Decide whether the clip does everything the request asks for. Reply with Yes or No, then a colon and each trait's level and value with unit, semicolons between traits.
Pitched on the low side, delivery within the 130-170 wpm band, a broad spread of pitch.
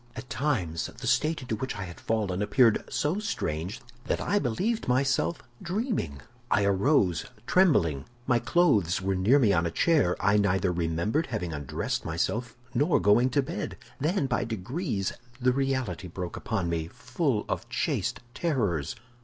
Yes: low, 115 Hz; average, 155 wpm; wide, 7.3 semitones